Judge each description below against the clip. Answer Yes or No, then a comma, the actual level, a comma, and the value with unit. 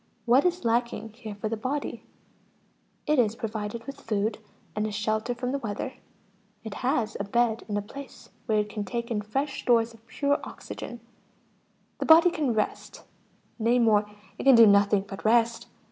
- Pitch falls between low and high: No, high, 230 Hz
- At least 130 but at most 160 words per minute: No, average, 175 wpm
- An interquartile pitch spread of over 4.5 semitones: No, average, 2.7 semitones